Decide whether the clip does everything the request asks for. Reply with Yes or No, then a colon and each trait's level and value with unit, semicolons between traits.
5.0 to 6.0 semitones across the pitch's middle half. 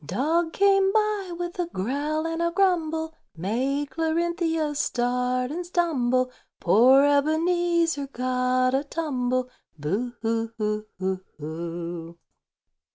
Yes: wide, 5.6 semitones